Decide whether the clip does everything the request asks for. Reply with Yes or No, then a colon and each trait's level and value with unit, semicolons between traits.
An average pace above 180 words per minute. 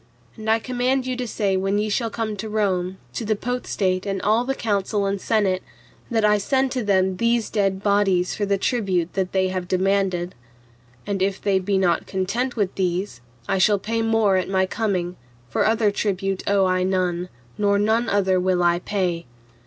Yes: average, 190 wpm